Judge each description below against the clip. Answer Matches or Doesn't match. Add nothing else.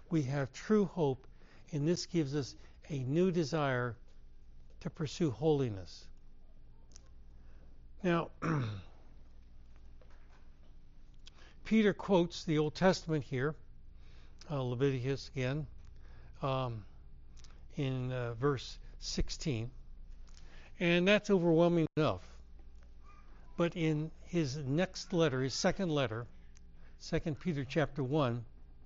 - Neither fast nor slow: Doesn't match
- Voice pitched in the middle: Doesn't match